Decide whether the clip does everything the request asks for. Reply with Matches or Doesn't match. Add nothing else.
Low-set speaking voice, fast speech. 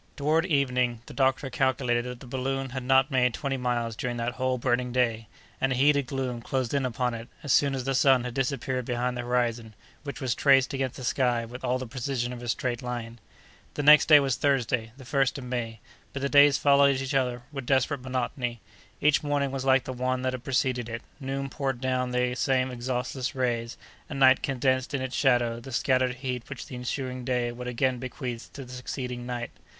Matches